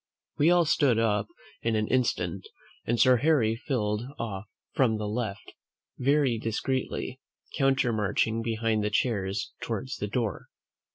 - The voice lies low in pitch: Yes, low, 115 Hz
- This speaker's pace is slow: Yes, slow, 130 wpm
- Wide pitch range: No, average, 3.4 semitones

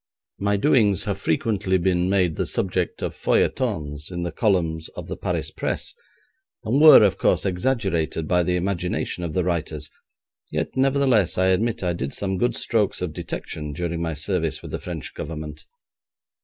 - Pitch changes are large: No, average, 3.7 semitones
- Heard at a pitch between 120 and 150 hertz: No, very low, 90 Hz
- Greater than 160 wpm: Yes, average, 170 wpm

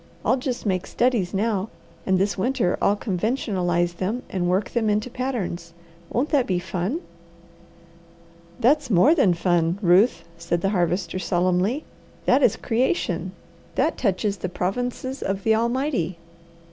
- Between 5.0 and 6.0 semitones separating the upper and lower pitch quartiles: Yes, wide, 5.5 semitones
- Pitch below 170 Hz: No, high, 195 Hz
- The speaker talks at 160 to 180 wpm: No, average, 140 wpm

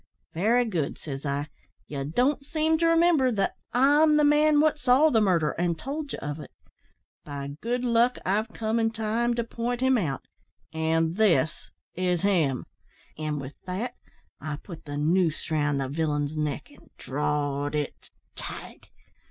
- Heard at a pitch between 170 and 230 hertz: Yes, medium, 185 Hz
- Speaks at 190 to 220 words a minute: No, average, 160 wpm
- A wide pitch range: Yes, wide, 8.8 semitones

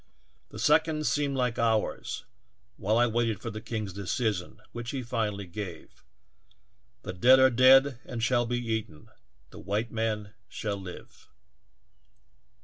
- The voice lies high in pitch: No, low, 115 Hz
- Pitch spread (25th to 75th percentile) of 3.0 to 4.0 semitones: Yes, average, 3.4 semitones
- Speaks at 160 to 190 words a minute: No, average, 150 wpm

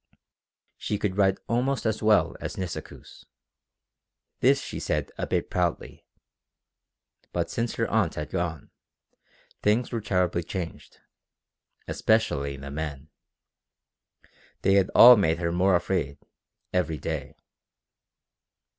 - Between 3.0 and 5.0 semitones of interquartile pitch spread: Yes, average, 4.7 semitones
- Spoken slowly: Yes, slow, 110 wpm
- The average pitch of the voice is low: Yes, very low, 90 Hz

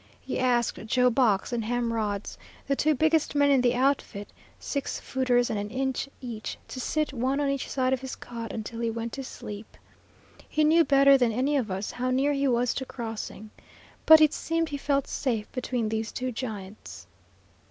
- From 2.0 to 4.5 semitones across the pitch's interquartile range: Yes, average, 3.3 semitones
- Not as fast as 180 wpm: No, average, 195 wpm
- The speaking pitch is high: Yes, very high, 255 Hz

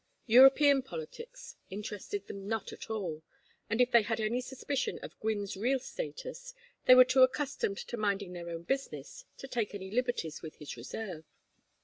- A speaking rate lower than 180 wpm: Yes, average, 165 wpm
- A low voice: No, high, 225 Hz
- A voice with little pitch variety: No, average, 5.1 semitones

